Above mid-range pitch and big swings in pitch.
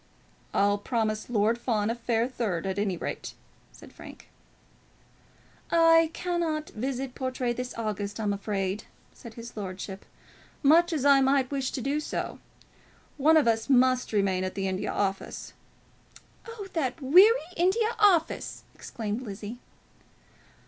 Yes: high, 245 Hz; wide, 6.0 semitones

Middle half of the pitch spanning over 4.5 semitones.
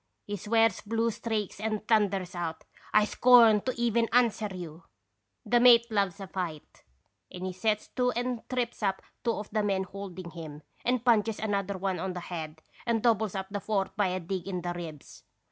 No: average, 3.7 semitones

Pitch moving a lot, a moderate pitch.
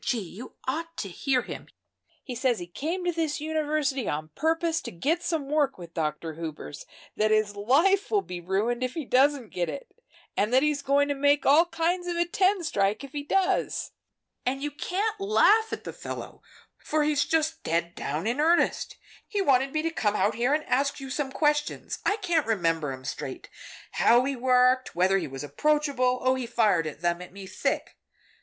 No: wide, 7.4 semitones; very high, 270 Hz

